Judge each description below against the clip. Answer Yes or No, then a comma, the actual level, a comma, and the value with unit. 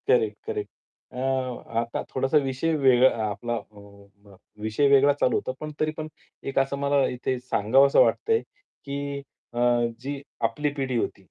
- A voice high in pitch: No, medium, 140 Hz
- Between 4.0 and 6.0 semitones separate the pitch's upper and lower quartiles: No, average, 2.7 semitones